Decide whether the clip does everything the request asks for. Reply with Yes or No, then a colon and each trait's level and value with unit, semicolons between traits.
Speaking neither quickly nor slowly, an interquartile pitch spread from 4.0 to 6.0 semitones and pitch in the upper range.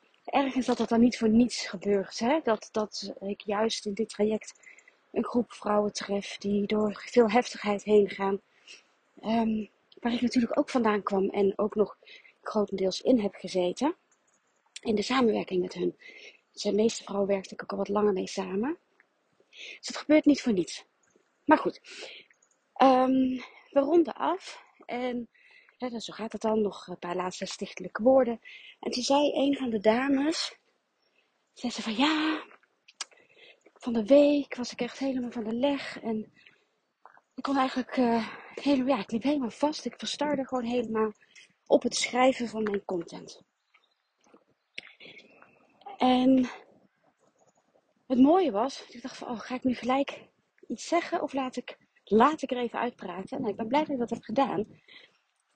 Yes: average, 170 wpm; average, 4.7 semitones; high, 245 Hz